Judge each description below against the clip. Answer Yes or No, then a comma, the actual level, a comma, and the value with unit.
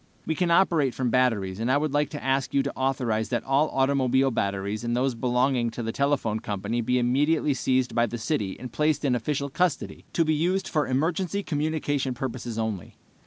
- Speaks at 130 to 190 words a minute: No, average, 200 wpm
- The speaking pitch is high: No, low, 130 Hz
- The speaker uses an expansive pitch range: No, average, 3.9 semitones